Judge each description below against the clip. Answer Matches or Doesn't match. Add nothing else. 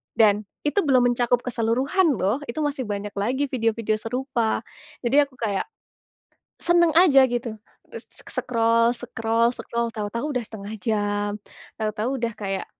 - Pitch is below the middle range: Doesn't match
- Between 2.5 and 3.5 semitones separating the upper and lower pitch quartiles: Matches